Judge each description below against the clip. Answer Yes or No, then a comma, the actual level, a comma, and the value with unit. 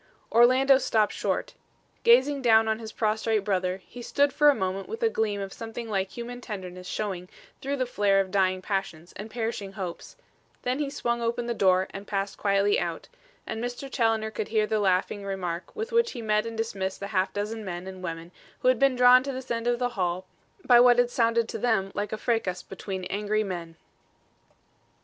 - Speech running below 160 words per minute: No, average, 200 wpm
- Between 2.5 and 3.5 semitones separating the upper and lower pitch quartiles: No, average, 3.9 semitones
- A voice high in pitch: Yes, high, 215 Hz